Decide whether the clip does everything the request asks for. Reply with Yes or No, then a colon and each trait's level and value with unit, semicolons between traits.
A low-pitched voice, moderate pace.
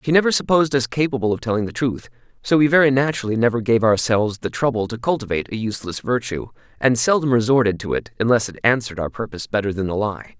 No: low, 120 Hz; fast, 215 wpm